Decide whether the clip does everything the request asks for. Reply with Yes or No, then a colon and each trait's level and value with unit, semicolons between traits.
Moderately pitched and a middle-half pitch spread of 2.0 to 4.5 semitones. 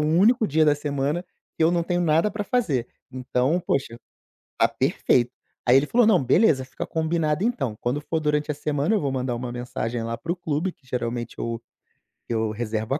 No: medium, 145 Hz; average, 5.3 semitones